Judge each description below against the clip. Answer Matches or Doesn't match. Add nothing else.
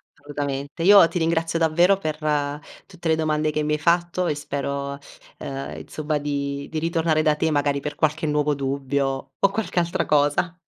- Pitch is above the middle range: Doesn't match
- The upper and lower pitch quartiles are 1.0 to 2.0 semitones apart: Doesn't match